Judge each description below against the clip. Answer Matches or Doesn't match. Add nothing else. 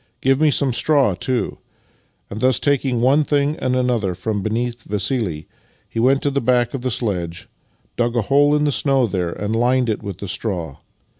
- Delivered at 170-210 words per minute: Matches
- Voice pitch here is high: Doesn't match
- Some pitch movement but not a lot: Matches